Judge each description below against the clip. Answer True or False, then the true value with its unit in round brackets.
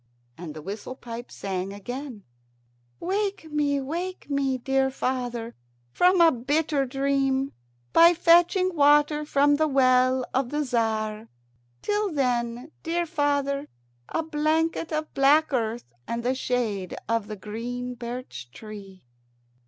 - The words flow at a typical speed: False (130 wpm)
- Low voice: False (270 Hz)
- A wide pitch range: False (4.4 semitones)